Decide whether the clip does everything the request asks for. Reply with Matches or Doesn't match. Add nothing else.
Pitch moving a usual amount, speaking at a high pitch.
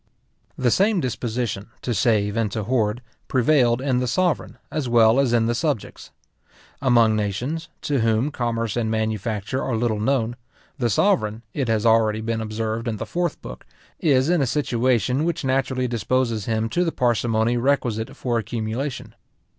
Doesn't match